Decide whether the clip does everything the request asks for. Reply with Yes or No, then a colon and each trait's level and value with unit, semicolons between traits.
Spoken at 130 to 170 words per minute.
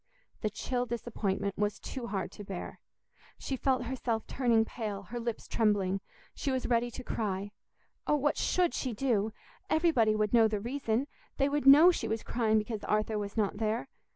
No: average, 180 wpm